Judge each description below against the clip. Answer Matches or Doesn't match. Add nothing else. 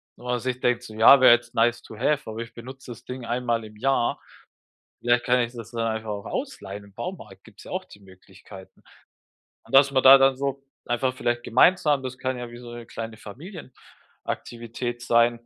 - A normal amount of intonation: Doesn't match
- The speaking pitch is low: Matches